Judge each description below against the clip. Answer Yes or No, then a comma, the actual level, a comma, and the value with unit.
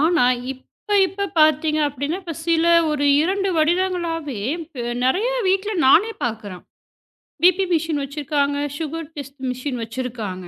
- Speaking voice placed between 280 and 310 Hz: Yes, very high, 305 Hz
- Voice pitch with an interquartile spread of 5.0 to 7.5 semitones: No, average, 4.6 semitones